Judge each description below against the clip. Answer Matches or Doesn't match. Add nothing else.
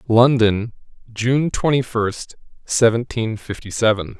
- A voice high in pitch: Doesn't match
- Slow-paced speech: Matches